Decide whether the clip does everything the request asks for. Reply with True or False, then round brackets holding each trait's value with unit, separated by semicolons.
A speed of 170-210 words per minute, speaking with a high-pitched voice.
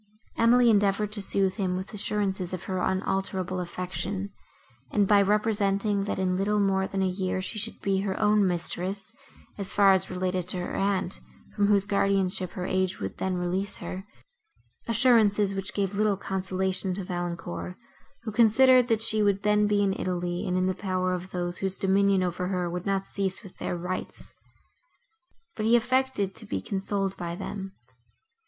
True (175 wpm; 195 Hz)